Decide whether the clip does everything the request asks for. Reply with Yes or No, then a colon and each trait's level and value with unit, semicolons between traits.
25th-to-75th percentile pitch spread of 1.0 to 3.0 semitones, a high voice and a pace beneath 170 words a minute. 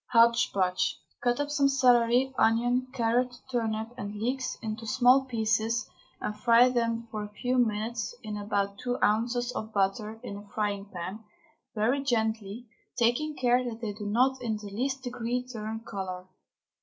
Yes: average, 2.7 semitones; high, 230 Hz; average, 160 wpm